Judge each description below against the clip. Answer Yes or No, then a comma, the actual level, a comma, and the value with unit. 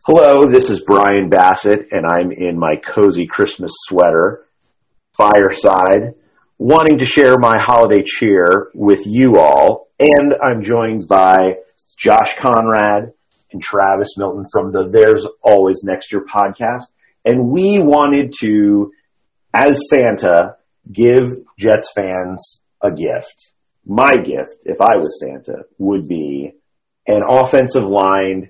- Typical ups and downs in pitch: Yes, average, 4.8 semitones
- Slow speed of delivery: Yes, slow, 125 wpm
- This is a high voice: No, low, 105 Hz